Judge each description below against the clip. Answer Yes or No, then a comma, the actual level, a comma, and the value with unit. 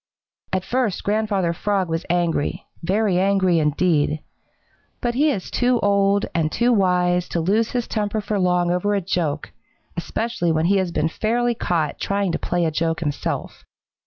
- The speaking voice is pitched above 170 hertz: Yes, medium, 185 Hz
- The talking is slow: No, average, 165 wpm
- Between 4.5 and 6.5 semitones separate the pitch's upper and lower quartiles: No, average, 3.7 semitones